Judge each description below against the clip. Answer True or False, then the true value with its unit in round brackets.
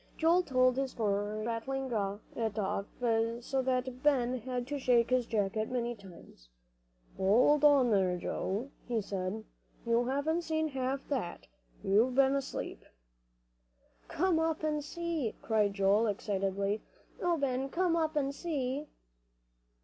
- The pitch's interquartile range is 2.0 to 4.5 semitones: False (4.9 semitones)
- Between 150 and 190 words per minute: False (135 wpm)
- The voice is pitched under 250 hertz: False (255 Hz)